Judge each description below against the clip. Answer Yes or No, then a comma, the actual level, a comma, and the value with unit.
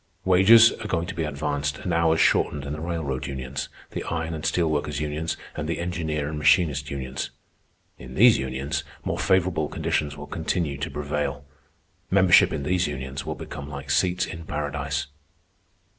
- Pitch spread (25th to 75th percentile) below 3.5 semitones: Yes, average, 2.9 semitones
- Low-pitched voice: Yes, very low, 75 Hz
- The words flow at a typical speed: Yes, average, 170 wpm